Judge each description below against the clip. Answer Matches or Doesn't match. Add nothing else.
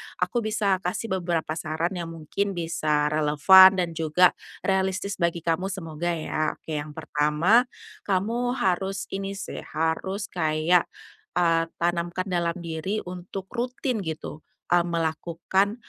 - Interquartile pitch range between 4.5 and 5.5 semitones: Doesn't match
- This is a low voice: Doesn't match